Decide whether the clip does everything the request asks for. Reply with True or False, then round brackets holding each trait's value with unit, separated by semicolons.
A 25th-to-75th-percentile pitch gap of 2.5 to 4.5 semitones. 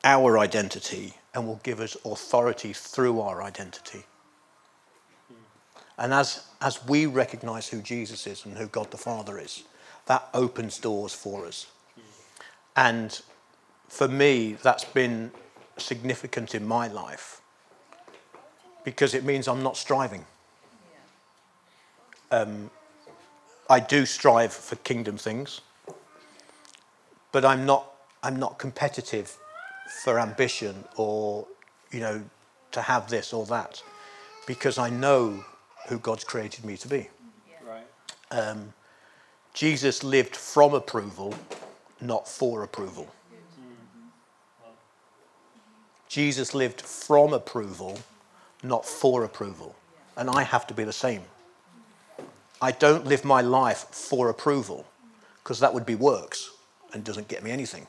True (3.8 semitones)